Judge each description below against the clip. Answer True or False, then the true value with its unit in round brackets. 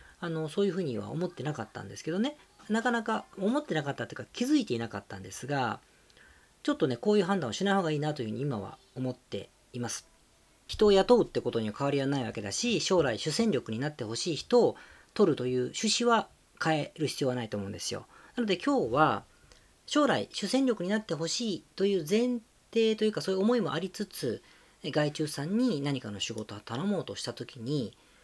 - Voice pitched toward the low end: False (160 Hz)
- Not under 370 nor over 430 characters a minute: True (425 characters per minute)